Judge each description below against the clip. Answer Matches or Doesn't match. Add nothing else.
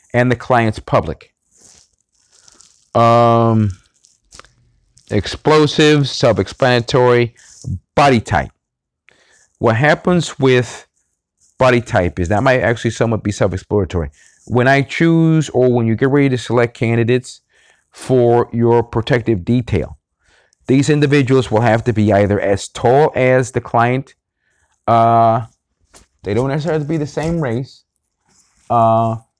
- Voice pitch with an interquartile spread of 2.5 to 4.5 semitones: Matches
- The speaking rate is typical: Doesn't match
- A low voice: Matches